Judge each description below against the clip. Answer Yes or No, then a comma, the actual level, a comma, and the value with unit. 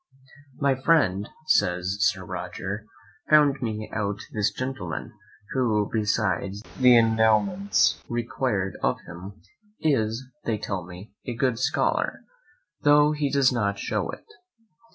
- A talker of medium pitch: No, low, 110 Hz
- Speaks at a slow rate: Yes, slow, 120 wpm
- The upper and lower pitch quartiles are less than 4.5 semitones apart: No, average, 4.8 semitones